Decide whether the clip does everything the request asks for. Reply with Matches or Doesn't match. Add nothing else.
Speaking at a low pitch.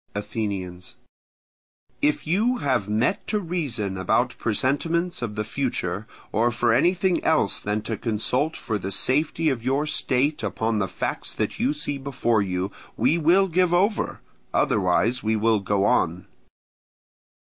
Matches